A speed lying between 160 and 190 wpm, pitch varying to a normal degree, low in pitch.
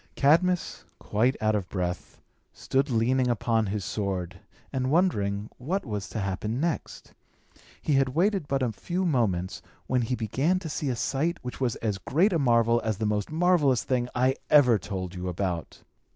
No: average, 175 wpm; wide, 5.7 semitones; low, 120 Hz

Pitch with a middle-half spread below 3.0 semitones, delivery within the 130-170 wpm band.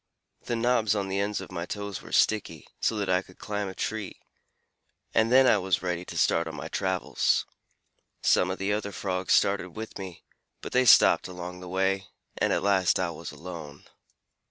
No: narrow, 2.4 semitones; average, 195 wpm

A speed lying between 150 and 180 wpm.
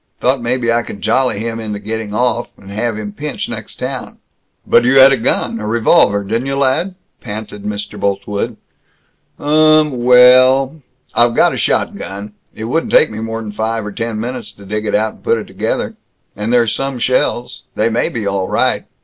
No: average, 190 wpm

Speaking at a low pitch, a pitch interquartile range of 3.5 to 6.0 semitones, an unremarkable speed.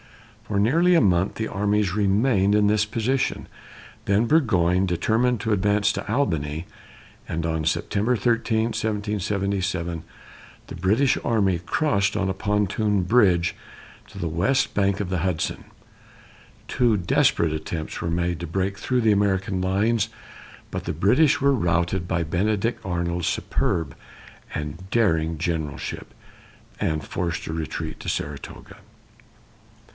No: low, 100 Hz; average, 4.2 semitones; slow, 130 wpm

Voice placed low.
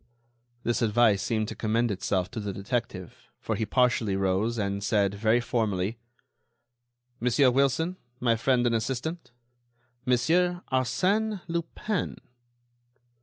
Yes: low, 120 Hz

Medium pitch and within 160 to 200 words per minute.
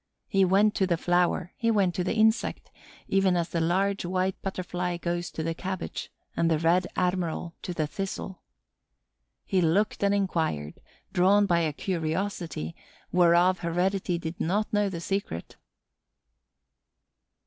No: medium, 180 Hz; average, 145 wpm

